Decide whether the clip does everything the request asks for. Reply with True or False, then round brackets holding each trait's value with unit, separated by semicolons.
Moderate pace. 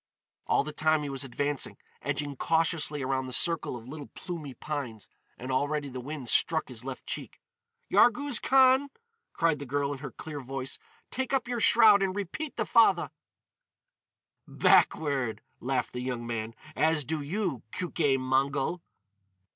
True (155 wpm)